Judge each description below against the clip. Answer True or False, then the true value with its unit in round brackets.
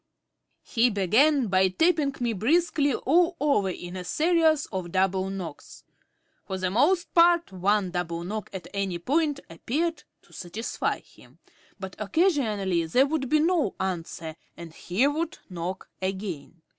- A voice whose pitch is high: True (210 Hz)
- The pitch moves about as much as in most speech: False (8.4 semitones)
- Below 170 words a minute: True (145 wpm)